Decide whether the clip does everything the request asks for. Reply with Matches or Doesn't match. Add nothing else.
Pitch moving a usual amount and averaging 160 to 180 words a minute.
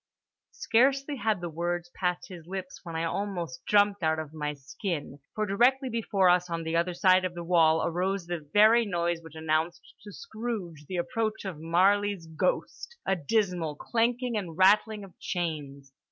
Matches